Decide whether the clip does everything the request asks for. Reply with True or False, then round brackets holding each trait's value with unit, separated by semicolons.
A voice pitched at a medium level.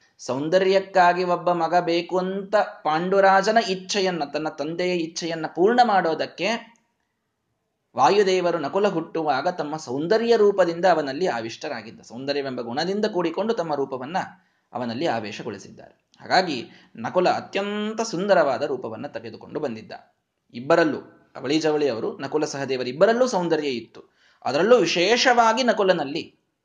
True (180 Hz)